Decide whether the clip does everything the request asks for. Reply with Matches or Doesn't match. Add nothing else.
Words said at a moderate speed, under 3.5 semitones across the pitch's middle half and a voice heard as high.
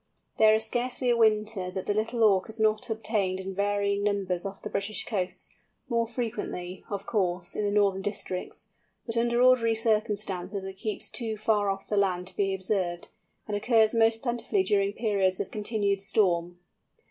Matches